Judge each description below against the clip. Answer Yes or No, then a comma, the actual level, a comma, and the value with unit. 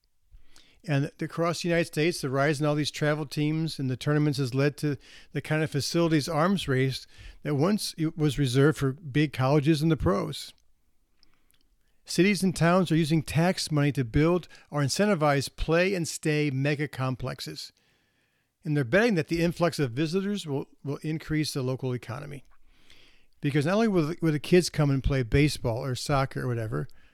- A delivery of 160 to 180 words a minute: Yes, average, 175 wpm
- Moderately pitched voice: Yes, medium, 150 Hz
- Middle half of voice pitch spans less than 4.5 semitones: Yes, average, 3.1 semitones